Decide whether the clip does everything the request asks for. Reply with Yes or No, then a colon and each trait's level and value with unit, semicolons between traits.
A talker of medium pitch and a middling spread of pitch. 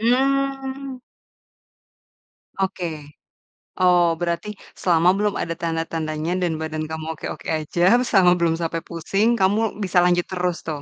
Yes: medium, 175 Hz; average, 4.0 semitones